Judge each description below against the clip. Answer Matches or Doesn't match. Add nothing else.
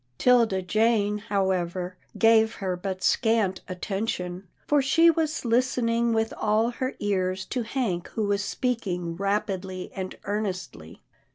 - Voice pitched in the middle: Doesn't match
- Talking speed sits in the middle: Doesn't match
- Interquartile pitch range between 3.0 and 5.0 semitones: Matches